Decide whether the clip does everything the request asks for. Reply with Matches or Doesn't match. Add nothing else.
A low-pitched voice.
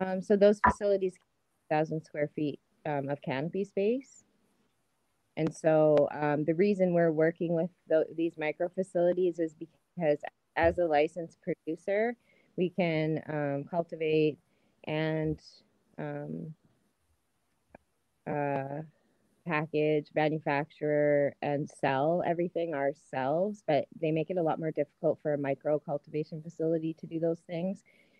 Doesn't match